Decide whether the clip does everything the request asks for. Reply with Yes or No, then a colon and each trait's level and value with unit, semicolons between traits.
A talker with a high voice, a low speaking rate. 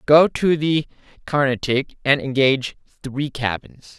No: medium, 140 Hz; slow, 120 wpm